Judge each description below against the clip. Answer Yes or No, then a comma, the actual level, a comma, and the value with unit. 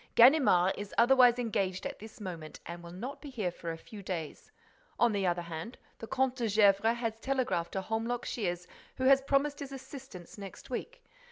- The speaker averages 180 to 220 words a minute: Yes, average, 190 wpm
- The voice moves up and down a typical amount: No, wide, 6.1 semitones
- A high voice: Yes, high, 220 Hz